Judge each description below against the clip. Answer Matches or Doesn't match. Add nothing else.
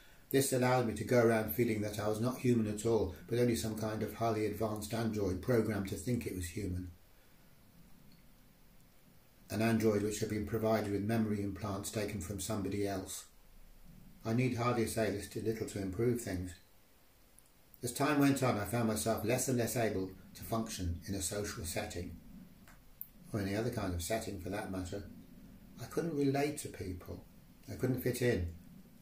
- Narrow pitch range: Doesn't match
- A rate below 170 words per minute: Doesn't match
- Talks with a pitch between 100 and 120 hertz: Matches